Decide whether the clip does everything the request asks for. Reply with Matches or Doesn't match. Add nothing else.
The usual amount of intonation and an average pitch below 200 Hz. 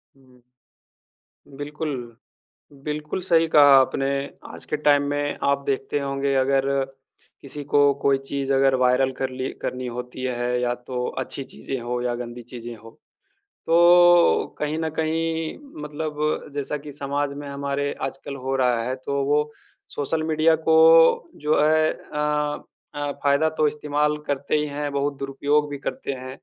Doesn't match